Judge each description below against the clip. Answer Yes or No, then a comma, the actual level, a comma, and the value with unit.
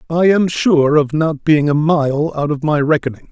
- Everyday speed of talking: No, fast, 215 wpm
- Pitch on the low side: No, medium, 150 Hz